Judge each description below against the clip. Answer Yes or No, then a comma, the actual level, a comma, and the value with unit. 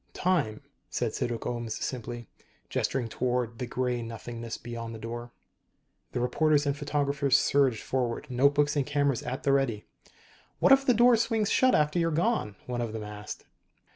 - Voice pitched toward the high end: No, low, 125 Hz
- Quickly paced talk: No, average, 165 wpm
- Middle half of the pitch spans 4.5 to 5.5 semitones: No, average, 3.9 semitones